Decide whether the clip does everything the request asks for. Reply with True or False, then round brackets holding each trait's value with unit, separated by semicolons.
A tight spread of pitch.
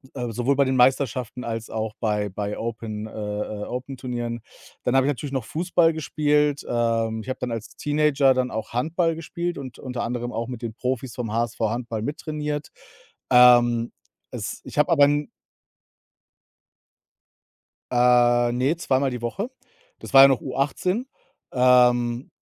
False (3.2 semitones)